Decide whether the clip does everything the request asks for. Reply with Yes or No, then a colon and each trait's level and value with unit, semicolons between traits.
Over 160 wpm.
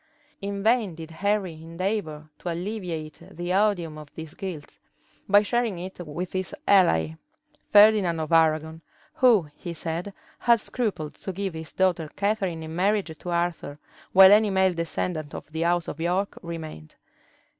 No: average, 155 wpm